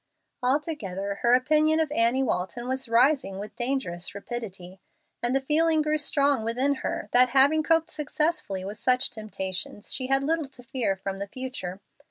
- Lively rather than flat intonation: Yes, wide, 6.1 semitones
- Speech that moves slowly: No, average, 165 wpm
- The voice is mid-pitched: No, very high, 255 Hz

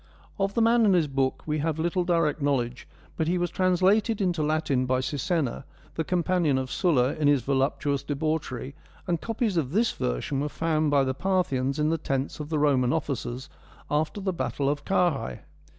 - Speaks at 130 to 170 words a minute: No, average, 185 wpm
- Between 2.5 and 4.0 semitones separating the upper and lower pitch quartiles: No, average, 4.4 semitones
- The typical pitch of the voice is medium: Yes, medium, 150 Hz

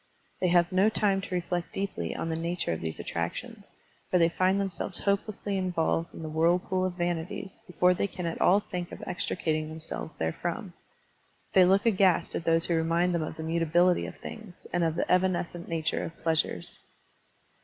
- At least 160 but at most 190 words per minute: Yes, average, 185 wpm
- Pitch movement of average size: No, narrow, 2.2 semitones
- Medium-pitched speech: Yes, medium, 175 Hz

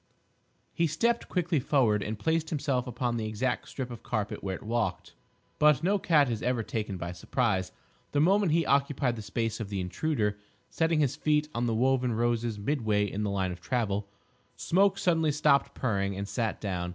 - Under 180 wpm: No, average, 190 wpm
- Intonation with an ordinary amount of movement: No, wide, 6.3 semitones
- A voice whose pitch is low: Yes, low, 120 Hz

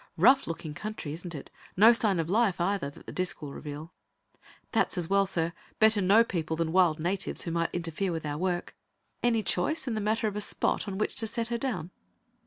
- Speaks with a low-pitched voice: No, medium, 185 Hz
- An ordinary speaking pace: No, fast, 215 wpm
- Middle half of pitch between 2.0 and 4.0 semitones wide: No, average, 4.6 semitones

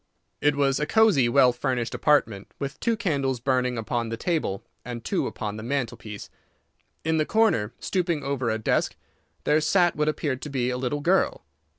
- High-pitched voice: No, low, 135 Hz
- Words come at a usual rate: Yes, average, 180 wpm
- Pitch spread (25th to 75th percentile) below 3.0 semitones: No, average, 4.2 semitones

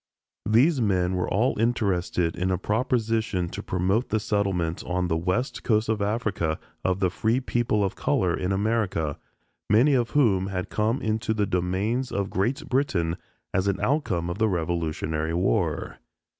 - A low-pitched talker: Yes, low, 100 Hz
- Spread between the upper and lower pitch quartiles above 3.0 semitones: Yes, average, 4.1 semitones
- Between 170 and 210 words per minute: No, average, 160 wpm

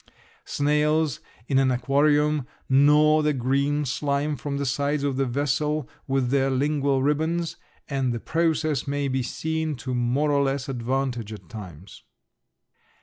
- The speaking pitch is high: No, medium, 140 Hz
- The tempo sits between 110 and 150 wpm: Yes, average, 145 wpm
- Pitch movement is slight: Yes, narrow, 2.3 semitones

